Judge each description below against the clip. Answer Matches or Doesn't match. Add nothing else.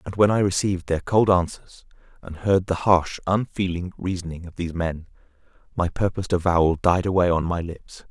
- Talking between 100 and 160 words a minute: Doesn't match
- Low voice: Matches